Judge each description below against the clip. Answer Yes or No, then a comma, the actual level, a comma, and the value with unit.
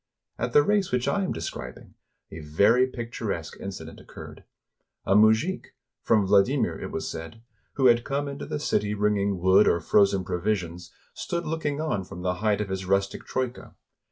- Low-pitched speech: Yes, low, 105 Hz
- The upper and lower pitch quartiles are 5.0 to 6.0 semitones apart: Yes, wide, 5.4 semitones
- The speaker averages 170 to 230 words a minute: Yes, average, 180 wpm